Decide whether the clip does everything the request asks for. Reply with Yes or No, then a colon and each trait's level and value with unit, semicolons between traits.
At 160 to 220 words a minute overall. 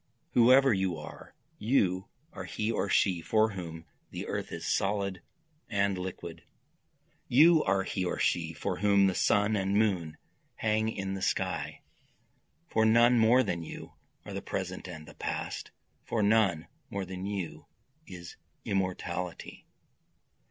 No: average, 145 wpm